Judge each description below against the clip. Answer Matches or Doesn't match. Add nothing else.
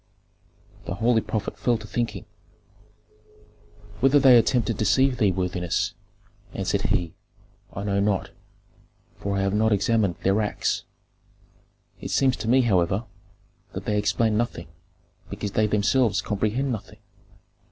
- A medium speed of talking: Doesn't match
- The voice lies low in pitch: Matches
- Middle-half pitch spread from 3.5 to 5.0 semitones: Doesn't match